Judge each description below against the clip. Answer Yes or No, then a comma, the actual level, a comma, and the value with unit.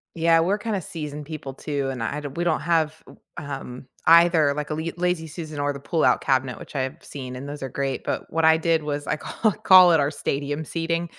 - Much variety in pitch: No, average, 2.8 semitones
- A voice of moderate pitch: Yes, medium, 155 Hz